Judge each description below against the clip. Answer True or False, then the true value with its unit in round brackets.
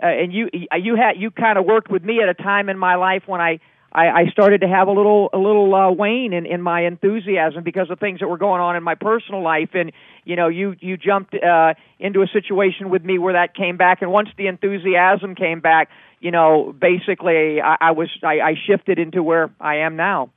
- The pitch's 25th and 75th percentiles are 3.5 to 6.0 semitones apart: False (2.8 semitones)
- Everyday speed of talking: False (240 wpm)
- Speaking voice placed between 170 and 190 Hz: True (185 Hz)